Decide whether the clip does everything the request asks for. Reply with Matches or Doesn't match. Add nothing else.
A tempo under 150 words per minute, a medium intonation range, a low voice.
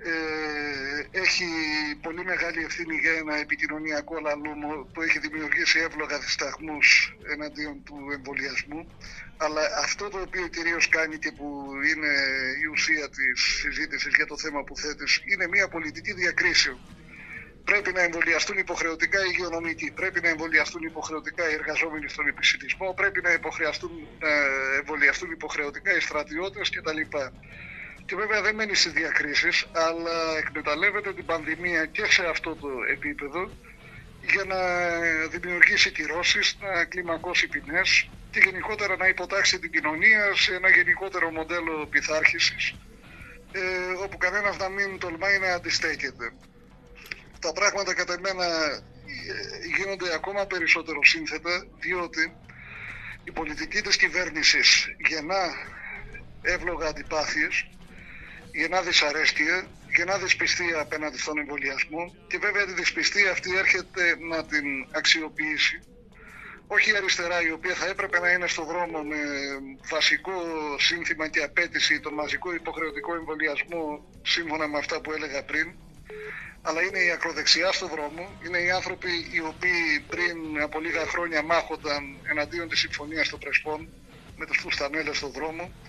Doesn't match